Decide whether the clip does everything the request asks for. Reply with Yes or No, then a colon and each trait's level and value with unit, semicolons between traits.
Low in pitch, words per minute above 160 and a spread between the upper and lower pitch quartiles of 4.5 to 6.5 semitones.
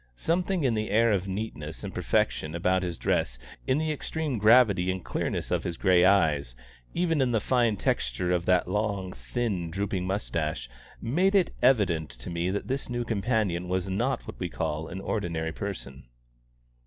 Yes: very low, 95 Hz; average, 175 wpm; wide, 5.5 semitones